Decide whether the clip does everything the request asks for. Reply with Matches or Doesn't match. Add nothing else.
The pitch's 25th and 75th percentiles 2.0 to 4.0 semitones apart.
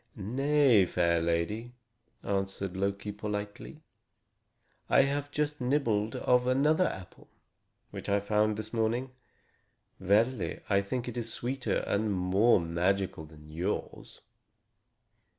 Doesn't match